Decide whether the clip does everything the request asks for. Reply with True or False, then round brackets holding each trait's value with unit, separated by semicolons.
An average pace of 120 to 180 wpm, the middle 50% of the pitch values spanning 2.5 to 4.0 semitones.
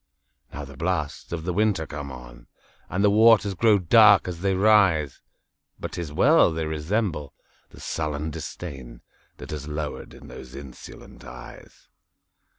False (135 wpm; 5.2 semitones)